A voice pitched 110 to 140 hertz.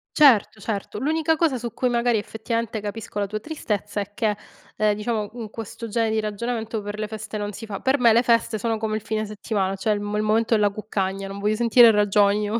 No: high, 215 Hz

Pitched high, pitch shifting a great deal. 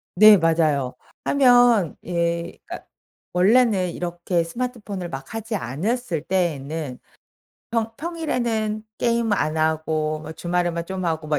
No: medium, 180 Hz; wide, 5.9 semitones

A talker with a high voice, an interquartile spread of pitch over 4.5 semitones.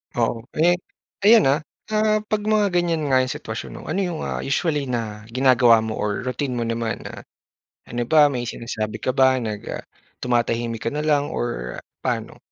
No: low, 130 Hz; average, 5.3 semitones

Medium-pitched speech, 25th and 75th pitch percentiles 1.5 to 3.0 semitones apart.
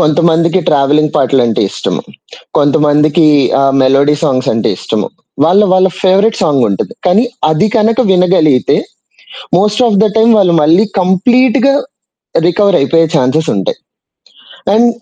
No: medium, 165 Hz; wide, 5.5 semitones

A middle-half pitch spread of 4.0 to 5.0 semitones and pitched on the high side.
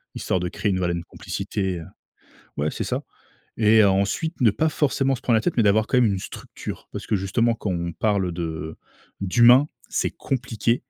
No: average, 4.7 semitones; low, 105 Hz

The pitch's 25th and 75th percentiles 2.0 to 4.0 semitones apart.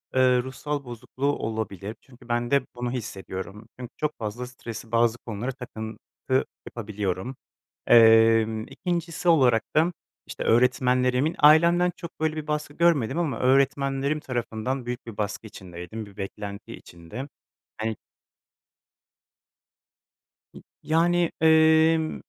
No: average, 5.2 semitones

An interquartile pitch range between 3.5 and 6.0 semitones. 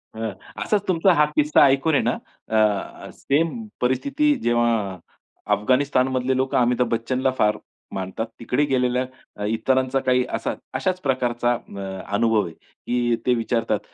No: average, 3.1 semitones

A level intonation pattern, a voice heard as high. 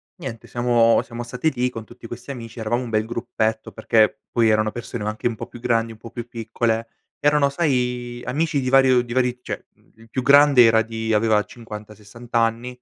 No: narrow, 1.8 semitones; low, 120 Hz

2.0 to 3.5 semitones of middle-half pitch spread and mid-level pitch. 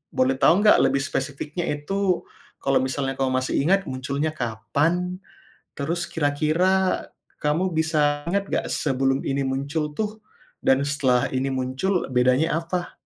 No: average, 4.5 semitones; medium, 145 Hz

